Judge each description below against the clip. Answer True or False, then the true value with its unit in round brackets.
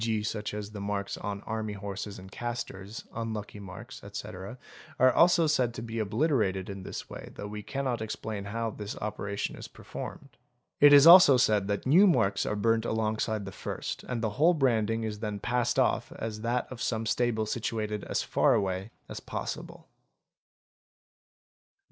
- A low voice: True (110 Hz)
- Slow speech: False (180 wpm)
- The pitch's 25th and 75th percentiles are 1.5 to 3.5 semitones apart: True (2.8 semitones)